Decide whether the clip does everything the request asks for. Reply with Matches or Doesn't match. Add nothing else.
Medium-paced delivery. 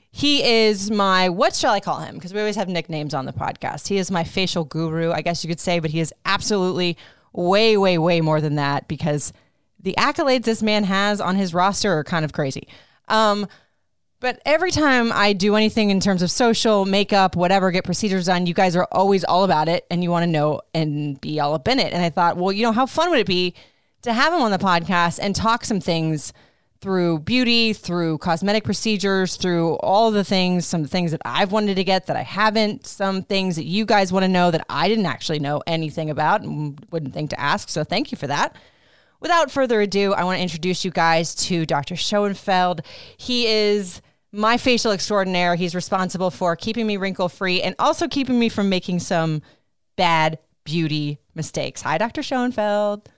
Doesn't match